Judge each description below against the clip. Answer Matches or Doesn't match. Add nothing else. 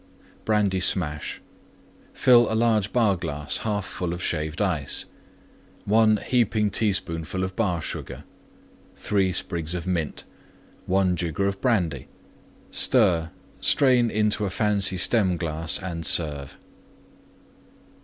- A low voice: Matches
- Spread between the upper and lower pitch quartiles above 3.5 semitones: Matches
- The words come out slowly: Matches